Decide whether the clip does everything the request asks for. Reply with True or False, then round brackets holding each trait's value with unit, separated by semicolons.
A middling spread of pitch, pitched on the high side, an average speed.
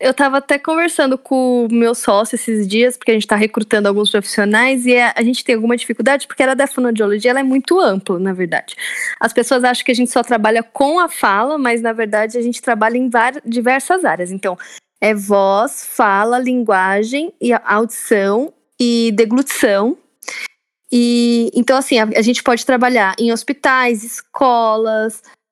True (3.0 semitones; 240 Hz; 170 wpm)